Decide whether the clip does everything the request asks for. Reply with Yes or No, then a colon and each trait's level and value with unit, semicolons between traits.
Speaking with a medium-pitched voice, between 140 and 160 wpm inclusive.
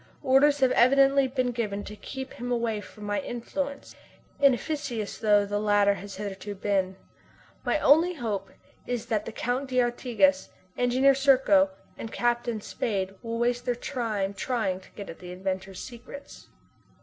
No: high, 235 Hz; average, 150 wpm